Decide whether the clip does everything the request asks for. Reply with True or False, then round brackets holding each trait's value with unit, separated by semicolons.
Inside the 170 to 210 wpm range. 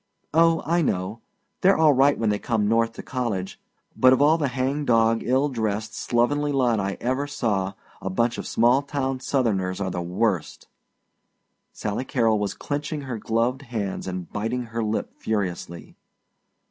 False (160 wpm)